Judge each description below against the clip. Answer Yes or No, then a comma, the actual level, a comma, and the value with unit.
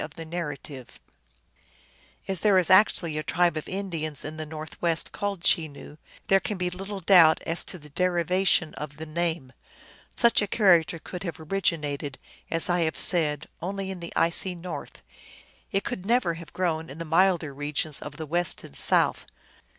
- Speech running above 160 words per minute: Yes, average, 170 wpm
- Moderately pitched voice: Yes, medium, 170 Hz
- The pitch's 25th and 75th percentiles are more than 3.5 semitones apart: No, average, 3.0 semitones